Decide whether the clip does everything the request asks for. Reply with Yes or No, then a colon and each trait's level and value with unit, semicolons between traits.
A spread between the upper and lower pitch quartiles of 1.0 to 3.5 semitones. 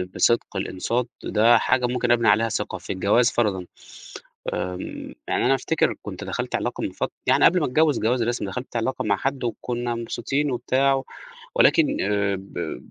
No: average, 4.0 semitones